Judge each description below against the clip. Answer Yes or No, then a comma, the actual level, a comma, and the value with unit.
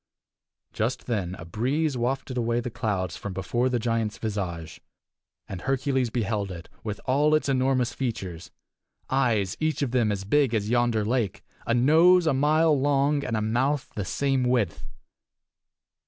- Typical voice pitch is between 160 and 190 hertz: No, low, 120 Hz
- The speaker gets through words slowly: No, average, 155 wpm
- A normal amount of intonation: Yes, average, 4.3 semitones